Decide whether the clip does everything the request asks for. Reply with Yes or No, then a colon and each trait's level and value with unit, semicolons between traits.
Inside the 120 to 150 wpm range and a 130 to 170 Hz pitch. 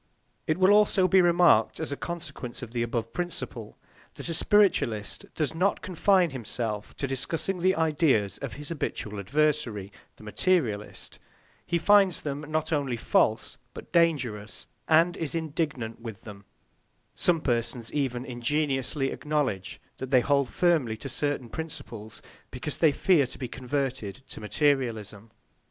Yes: average, 145 wpm; medium, 140 Hz